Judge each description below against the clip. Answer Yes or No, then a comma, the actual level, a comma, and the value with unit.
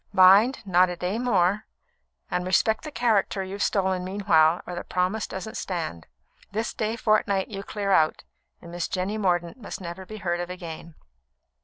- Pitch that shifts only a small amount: No, average, 3.1 semitones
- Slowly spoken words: No, average, 170 wpm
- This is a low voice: No, high, 190 Hz